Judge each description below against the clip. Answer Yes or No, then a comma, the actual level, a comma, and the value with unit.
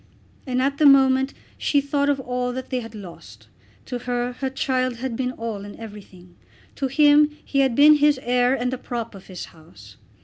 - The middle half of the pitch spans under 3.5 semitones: Yes, average, 3.1 semitones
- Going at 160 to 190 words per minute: No, average, 200 wpm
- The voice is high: Yes, very high, 250 Hz